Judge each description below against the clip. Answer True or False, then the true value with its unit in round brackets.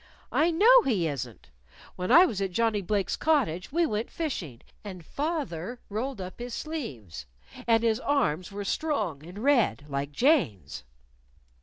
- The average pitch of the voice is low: False (215 Hz)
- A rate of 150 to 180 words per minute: True (155 wpm)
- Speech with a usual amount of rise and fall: False (9.0 semitones)